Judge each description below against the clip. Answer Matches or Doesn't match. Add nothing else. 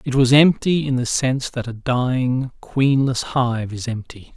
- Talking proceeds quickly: Doesn't match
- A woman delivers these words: Doesn't match